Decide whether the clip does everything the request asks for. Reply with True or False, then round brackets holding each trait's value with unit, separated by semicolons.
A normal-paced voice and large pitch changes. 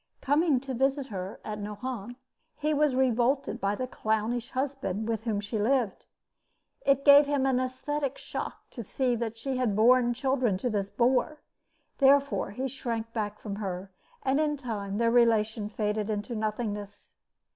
False (160 wpm; 4.0 semitones)